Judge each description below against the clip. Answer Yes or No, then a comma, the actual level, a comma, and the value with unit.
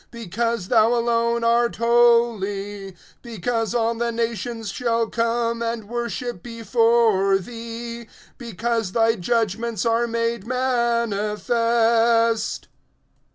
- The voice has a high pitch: Yes, high, 230 Hz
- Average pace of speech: No, slow, 95 wpm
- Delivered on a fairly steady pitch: Yes, narrow, 0.9 semitones